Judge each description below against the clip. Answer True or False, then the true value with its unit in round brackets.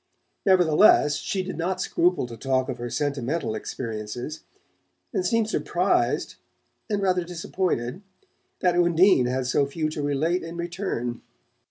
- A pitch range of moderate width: False (5.9 semitones)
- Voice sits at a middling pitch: True (160 Hz)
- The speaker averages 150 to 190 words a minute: False (135 wpm)